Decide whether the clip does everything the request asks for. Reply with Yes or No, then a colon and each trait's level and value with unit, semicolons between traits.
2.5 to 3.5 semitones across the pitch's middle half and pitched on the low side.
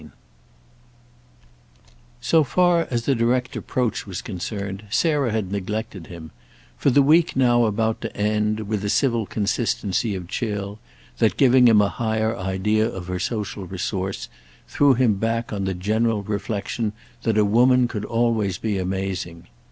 Yes: average, 3.2 semitones; low, 110 Hz